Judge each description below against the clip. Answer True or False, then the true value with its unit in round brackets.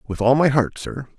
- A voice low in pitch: True (130 Hz)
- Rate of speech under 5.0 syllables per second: False (5.1 syllables/s)